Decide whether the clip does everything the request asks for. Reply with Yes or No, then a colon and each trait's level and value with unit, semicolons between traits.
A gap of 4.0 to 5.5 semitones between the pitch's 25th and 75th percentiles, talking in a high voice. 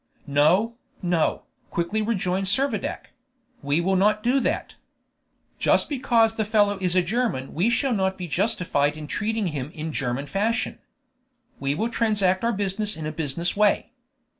Yes: average, 4.9 semitones; high, 195 Hz